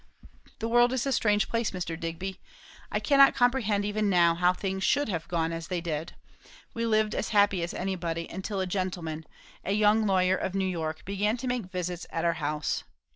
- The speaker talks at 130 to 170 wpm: No, average, 195 wpm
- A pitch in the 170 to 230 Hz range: Yes, high, 190 Hz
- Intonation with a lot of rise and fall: No, average, 4.0 semitones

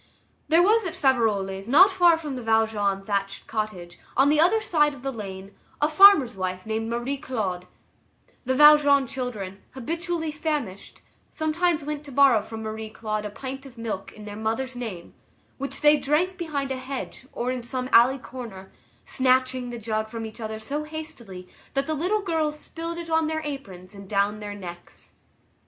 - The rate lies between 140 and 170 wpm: No, average, 180 wpm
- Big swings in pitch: Yes, wide, 5.9 semitones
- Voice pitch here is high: Yes, very high, 255 Hz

